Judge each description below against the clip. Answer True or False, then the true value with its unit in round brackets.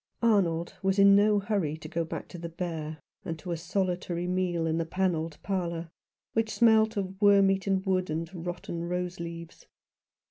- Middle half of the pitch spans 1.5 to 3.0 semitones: True (2.7 semitones)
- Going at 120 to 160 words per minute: False (170 wpm)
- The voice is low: False (180 Hz)